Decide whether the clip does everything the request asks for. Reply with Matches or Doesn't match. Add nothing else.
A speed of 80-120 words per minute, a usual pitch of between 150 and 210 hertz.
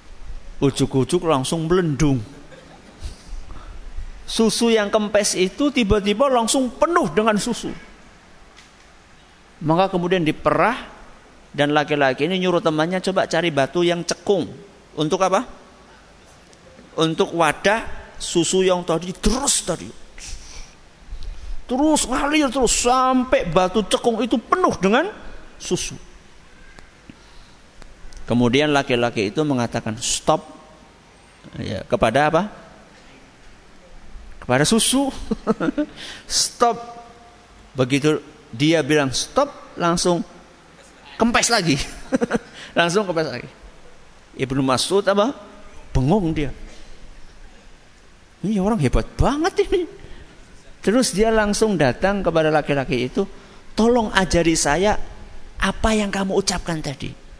Matches